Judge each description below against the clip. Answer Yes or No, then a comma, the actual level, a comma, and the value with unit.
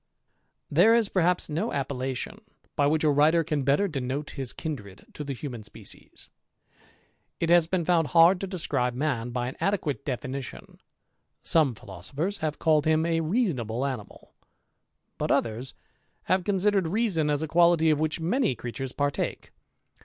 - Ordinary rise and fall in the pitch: Yes, average, 4.5 semitones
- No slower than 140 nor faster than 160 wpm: Yes, average, 155 wpm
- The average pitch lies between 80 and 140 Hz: No, medium, 150 Hz